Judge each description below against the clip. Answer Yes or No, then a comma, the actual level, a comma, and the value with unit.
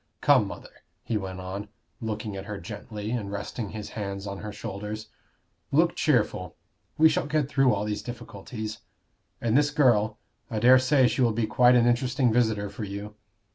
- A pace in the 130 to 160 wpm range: No, average, 175 wpm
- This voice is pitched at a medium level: No, low, 110 Hz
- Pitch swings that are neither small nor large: Yes, average, 3.3 semitones